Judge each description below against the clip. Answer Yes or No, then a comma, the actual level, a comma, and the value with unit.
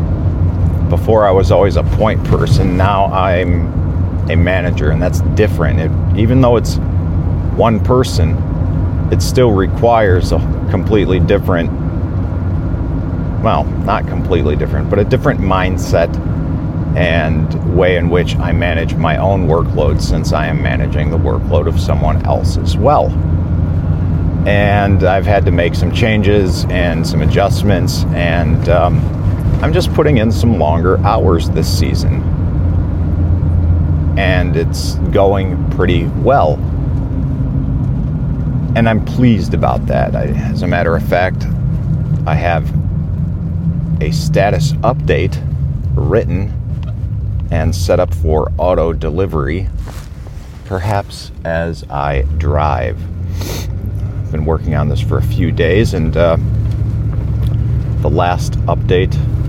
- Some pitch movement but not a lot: Yes, average, 3.3 semitones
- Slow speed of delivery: Yes, slow, 120 wpm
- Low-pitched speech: Yes, very low, 90 Hz